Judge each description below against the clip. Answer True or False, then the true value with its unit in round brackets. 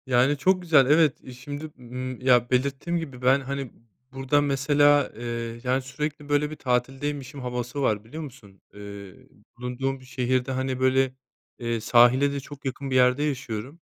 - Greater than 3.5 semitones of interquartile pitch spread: False (2.5 semitones)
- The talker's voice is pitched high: False (130 Hz)